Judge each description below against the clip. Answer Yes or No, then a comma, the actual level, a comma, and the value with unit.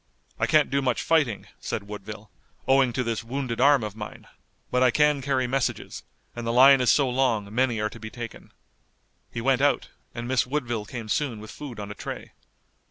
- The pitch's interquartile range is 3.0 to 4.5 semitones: Yes, average, 3.5 semitones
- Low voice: Yes, low, 125 Hz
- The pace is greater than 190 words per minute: Yes, average, 200 wpm